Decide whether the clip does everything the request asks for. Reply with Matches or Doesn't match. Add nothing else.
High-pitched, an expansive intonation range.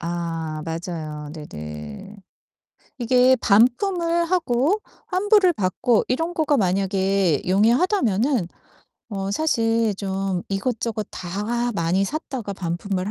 Matches